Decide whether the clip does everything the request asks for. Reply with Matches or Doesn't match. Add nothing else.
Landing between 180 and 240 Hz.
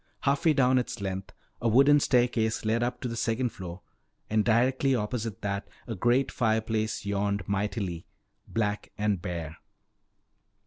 Doesn't match